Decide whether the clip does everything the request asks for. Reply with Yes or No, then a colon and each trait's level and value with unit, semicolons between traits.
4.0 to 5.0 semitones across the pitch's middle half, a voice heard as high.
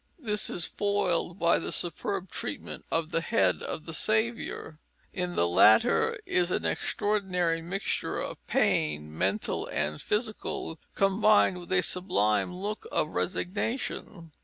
No: average, 4.5 semitones; medium, 180 Hz